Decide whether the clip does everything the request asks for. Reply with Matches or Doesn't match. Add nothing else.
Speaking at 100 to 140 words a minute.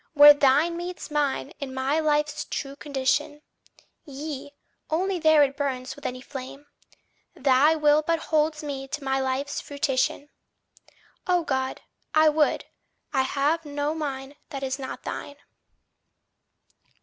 Matches